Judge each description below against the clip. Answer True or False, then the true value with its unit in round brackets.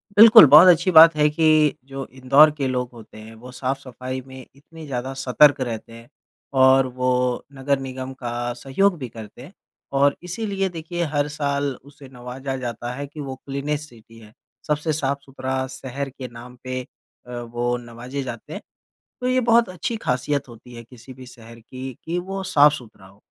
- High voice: False (135 Hz)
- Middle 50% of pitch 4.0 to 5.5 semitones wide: False (3.3 semitones)